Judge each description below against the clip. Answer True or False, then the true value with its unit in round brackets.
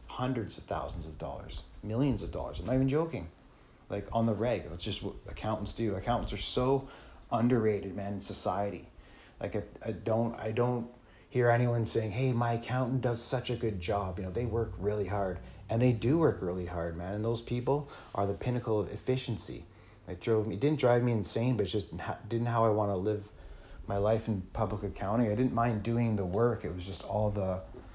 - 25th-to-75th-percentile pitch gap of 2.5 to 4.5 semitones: True (3.3 semitones)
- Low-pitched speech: True (110 Hz)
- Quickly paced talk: True (215 wpm)